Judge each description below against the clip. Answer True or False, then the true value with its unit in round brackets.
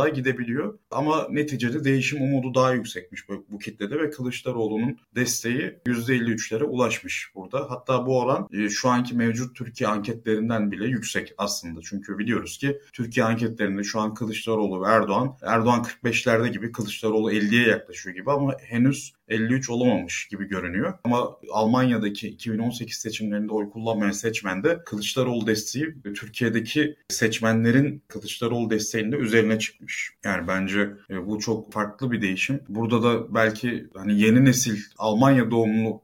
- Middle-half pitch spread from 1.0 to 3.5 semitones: True (2.7 semitones)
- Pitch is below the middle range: True (115 Hz)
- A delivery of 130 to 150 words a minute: True (135 wpm)